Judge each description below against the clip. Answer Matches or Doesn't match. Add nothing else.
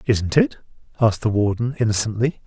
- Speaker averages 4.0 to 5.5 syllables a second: Doesn't match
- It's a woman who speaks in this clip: Doesn't match